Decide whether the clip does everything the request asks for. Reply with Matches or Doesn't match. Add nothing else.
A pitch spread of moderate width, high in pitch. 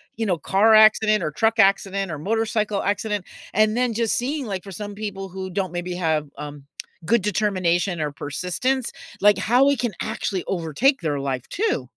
Matches